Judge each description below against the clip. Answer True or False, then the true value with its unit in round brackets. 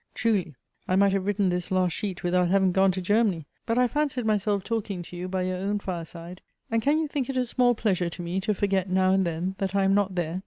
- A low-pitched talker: False (190 Hz)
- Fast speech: True (250 wpm)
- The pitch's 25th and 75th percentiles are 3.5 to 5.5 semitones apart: False (2.8 semitones)